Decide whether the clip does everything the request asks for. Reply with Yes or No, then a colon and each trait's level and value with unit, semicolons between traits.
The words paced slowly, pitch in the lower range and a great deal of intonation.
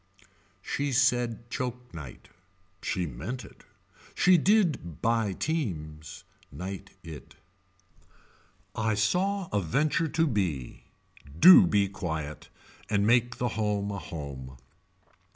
Yes: slow, 110 wpm; low, 105 Hz; wide, 8.2 semitones